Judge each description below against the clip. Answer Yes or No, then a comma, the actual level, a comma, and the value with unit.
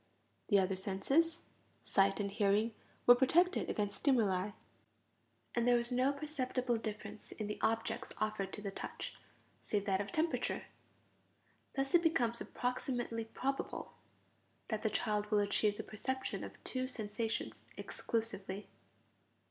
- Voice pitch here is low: No, high, 225 Hz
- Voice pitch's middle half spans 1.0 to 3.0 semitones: No, average, 3.8 semitones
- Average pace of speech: No, slow, 130 wpm